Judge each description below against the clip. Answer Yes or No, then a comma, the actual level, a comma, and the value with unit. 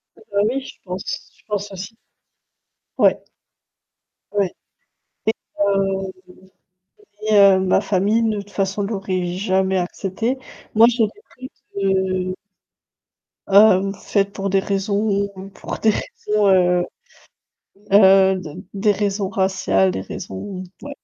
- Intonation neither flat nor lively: No, narrow, 1.7 semitones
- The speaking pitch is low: No, high, 195 Hz